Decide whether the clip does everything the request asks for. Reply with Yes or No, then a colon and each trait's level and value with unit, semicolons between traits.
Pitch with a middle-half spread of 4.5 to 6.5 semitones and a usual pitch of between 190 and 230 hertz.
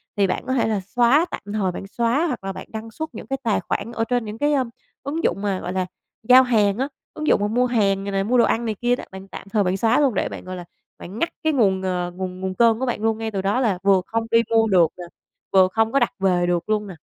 No: average, 3.9 semitones; high, 220 Hz